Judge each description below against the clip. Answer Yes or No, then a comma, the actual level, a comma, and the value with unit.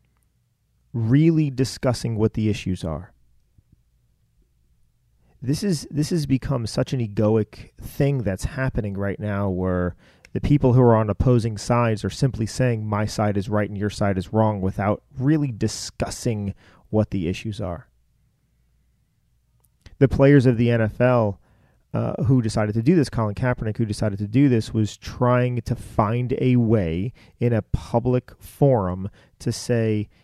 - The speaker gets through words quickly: No, average, 150 wpm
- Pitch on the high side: No, low, 110 Hz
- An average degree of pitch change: Yes, average, 4.0 semitones